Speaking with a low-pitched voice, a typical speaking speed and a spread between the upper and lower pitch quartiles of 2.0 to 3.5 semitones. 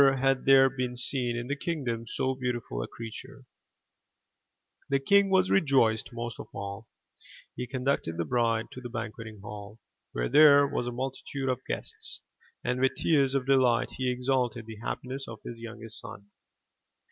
Yes: low, 125 Hz; average, 165 wpm; average, 2.9 semitones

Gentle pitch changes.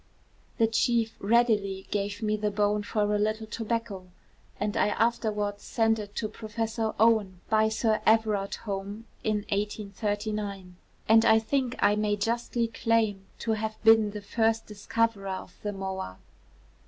Yes: narrow, 1.6 semitones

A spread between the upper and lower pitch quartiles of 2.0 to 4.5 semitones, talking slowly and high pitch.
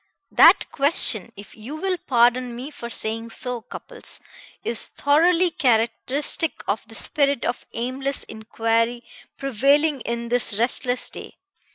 Yes: average, 3.6 semitones; slow, 130 wpm; high, 245 Hz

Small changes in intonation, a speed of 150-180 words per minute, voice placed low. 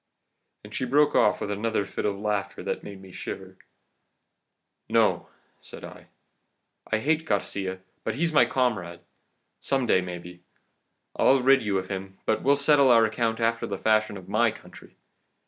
No: average, 4.8 semitones; average, 165 wpm; low, 110 Hz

